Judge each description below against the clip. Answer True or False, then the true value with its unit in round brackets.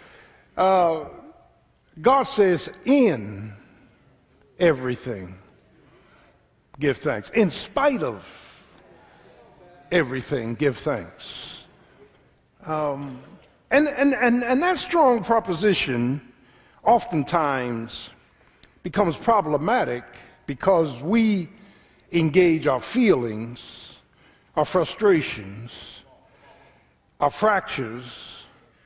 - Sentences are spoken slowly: True (70 wpm)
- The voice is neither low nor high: True (155 Hz)